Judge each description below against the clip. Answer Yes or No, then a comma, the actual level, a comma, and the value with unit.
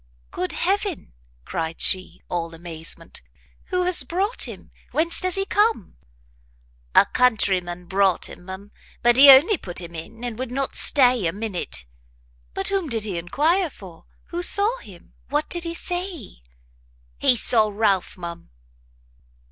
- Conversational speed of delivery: Yes, average, 150 wpm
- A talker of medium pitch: No, high, 235 Hz